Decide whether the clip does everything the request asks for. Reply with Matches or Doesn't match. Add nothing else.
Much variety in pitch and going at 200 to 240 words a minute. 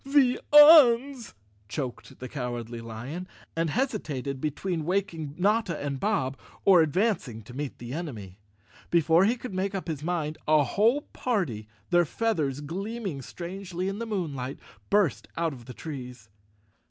Doesn't match